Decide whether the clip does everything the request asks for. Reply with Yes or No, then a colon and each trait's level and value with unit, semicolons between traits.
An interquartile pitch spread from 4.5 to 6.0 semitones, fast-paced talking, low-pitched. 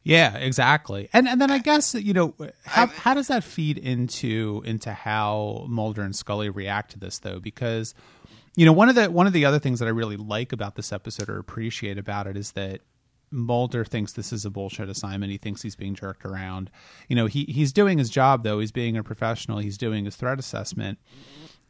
Yes: average, 5.3 semitones; fast, 215 wpm; low, 115 Hz